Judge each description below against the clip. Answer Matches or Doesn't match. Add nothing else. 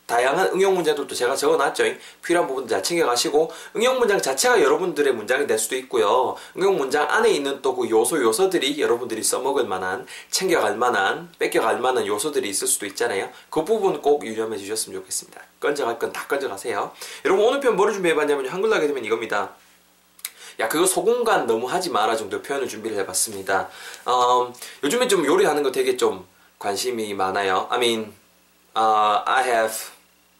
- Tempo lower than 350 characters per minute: Doesn't match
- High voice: Matches